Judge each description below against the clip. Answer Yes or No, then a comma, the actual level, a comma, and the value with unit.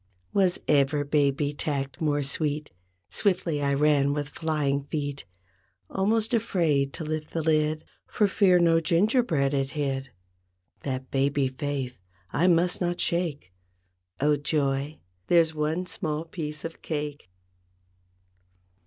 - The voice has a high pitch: No, medium, 150 Hz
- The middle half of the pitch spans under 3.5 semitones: Yes, average, 3.0 semitones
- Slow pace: Yes, slow, 125 wpm